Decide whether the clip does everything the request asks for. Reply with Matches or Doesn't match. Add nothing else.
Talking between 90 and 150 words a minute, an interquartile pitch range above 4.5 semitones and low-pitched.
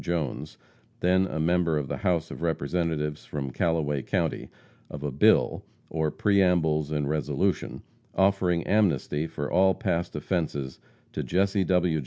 Doesn't match